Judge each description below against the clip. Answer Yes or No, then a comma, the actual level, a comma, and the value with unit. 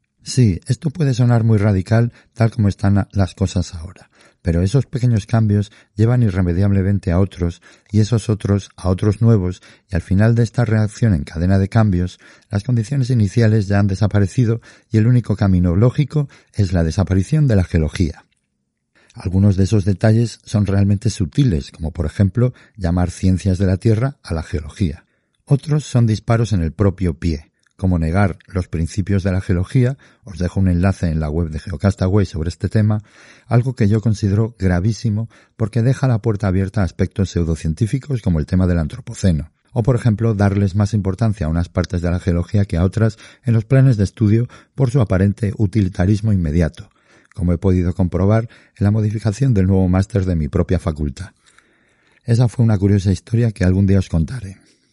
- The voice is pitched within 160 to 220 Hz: No, low, 100 Hz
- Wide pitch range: No, average, 3.7 semitones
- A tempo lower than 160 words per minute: No, average, 180 wpm